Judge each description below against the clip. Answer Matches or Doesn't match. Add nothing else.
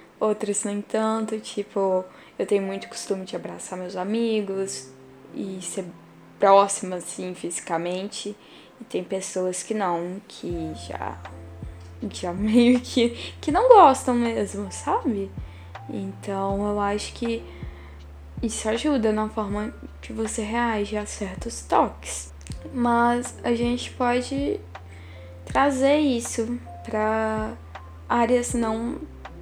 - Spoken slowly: Matches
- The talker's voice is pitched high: Matches